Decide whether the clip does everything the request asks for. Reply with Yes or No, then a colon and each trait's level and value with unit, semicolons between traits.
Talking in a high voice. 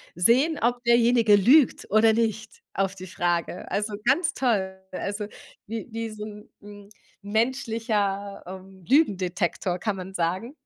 Yes: high, 210 Hz